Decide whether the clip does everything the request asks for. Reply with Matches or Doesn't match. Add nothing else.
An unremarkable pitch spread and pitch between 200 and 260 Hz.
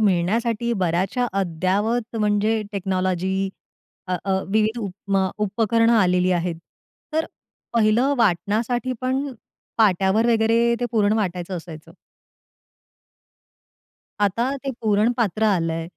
Matches